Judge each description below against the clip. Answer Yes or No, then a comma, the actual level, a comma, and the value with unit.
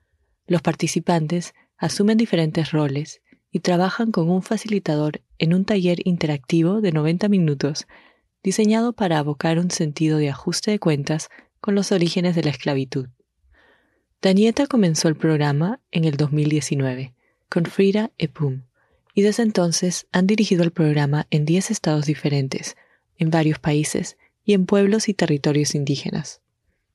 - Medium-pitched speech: Yes, medium, 170 Hz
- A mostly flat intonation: No, average, 4.3 semitones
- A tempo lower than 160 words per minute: Yes, average, 140 wpm